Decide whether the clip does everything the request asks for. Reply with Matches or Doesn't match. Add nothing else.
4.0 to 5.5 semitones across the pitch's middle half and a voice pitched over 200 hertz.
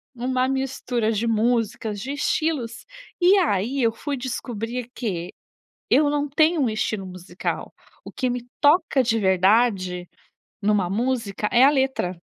Matches